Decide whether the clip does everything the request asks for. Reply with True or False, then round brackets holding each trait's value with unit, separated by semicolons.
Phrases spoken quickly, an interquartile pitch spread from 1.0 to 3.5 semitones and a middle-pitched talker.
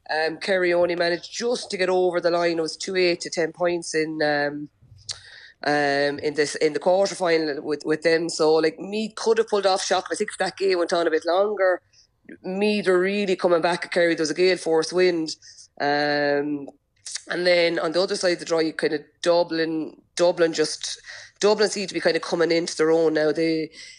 True (215 wpm; 2.9 semitones; 170 Hz)